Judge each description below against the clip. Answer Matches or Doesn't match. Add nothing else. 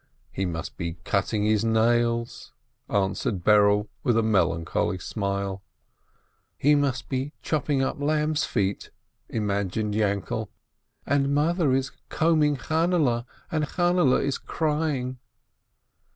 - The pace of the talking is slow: Matches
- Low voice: Matches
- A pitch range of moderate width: Doesn't match